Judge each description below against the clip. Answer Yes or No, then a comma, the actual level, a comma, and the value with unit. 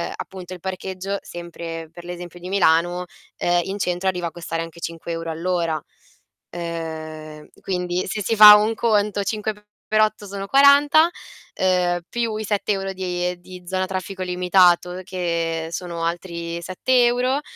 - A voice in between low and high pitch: Yes, medium, 180 Hz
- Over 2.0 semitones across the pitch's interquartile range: Yes, average, 2.7 semitones